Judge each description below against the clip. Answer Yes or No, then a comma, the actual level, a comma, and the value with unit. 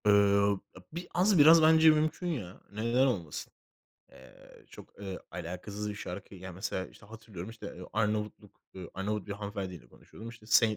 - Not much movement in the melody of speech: No, average, 3.6 semitones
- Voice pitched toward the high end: No, low, 105 Hz